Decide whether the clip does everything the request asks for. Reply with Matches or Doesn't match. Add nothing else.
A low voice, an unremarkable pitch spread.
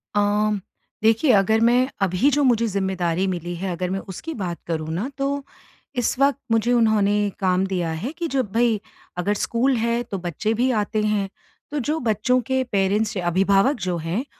Doesn't match